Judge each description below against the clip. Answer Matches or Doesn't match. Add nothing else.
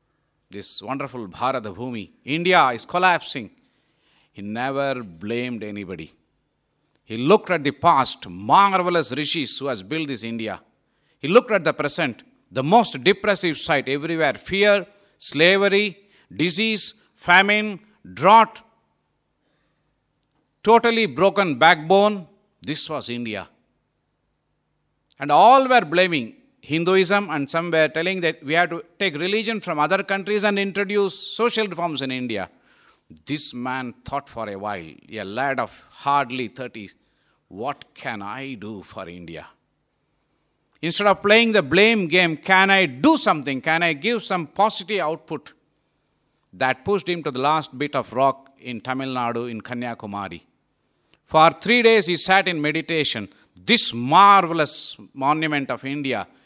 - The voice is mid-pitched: Matches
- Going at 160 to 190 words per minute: Doesn't match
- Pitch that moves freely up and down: Matches